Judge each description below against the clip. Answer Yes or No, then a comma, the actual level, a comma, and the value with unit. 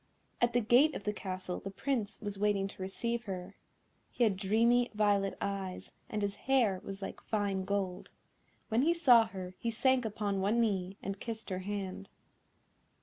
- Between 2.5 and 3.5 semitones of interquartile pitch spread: Yes, average, 3.2 semitones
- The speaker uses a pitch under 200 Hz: No, high, 205 Hz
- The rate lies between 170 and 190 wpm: Yes, average, 175 wpm